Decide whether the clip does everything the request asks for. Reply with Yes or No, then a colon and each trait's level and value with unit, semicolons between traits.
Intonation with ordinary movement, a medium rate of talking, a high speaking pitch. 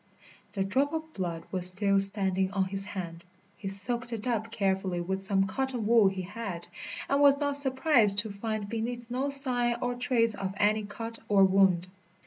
Yes: average, 4.0 semitones; average, 180 wpm; high, 210 Hz